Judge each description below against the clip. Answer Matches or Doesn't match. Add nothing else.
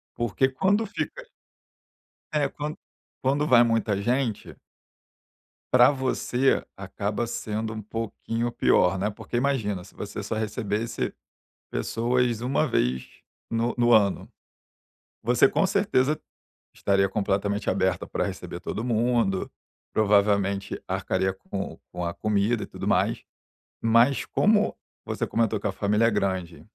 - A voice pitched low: Matches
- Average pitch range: Matches